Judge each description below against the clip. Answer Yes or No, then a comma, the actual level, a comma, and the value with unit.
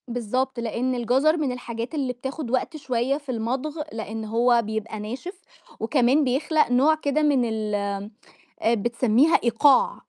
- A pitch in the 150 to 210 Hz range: No, very high, 250 Hz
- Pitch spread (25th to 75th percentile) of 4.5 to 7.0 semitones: No, average, 3.5 semitones